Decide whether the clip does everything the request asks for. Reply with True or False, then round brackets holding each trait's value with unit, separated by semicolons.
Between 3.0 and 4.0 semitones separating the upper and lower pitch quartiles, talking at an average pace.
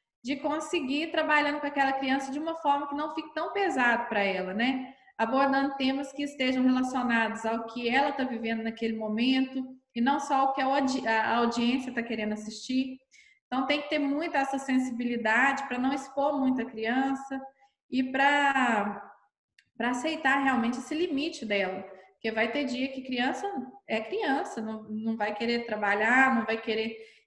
True (3.4 semitones; 175 wpm)